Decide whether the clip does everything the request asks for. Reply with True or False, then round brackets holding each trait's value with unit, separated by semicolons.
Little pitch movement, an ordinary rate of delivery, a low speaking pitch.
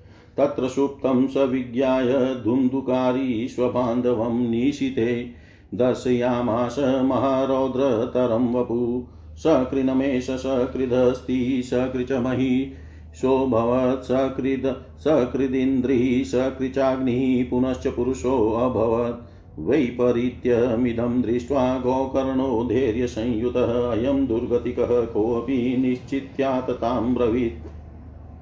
False (1.5 semitones; 55 wpm; 125 Hz)